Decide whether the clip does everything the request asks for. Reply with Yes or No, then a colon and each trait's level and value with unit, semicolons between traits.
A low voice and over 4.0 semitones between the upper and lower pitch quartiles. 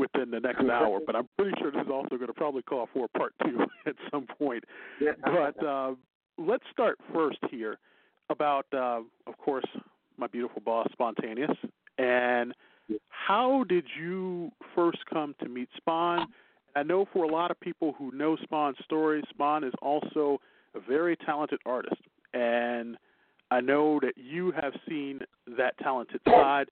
No: medium, 150 Hz; average, 4.9 semitones